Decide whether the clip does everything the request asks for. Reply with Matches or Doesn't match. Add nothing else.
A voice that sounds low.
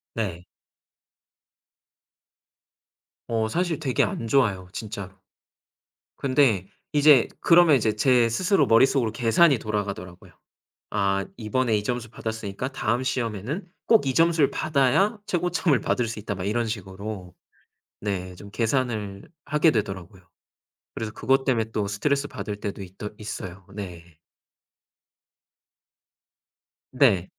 Matches